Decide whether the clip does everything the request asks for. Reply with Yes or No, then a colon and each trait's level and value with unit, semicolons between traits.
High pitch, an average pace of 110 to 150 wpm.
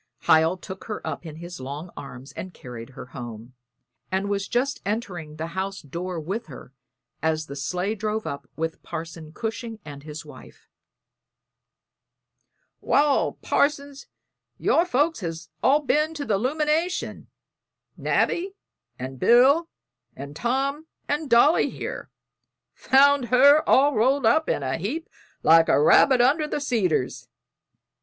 Yes: high, 200 Hz; slow, 135 wpm